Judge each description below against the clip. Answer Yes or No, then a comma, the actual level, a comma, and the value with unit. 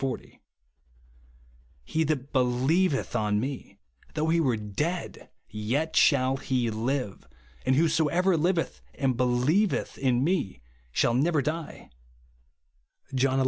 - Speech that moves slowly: Yes, slow, 125 wpm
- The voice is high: No, low, 130 Hz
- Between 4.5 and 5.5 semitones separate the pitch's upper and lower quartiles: Yes, average, 5.2 semitones